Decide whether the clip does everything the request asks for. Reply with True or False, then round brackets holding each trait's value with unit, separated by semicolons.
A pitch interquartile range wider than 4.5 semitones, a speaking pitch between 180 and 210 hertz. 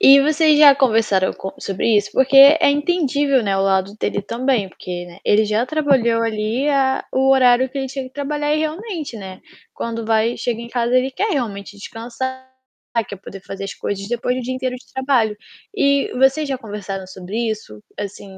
False (4.9 semitones; 245 Hz)